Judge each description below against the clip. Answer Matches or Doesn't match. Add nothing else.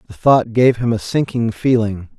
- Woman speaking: Doesn't match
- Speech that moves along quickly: Doesn't match